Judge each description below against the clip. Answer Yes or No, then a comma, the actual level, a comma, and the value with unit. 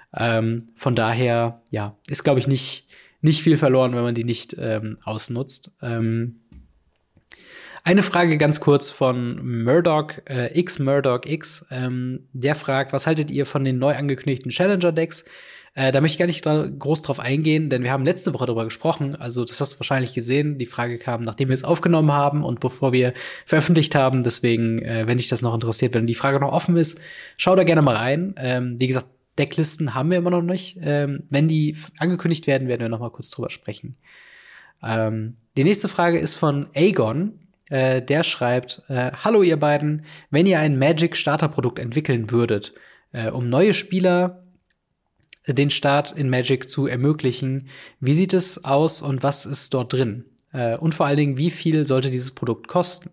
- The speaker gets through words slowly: No, average, 180 wpm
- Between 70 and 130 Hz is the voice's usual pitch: No, medium, 140 Hz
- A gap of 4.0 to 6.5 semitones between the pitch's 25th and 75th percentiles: Yes, average, 4.3 semitones